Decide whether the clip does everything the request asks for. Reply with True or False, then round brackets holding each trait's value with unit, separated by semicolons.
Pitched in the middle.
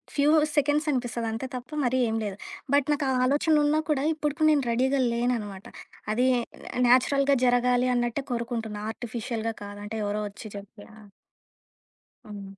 False (245 Hz)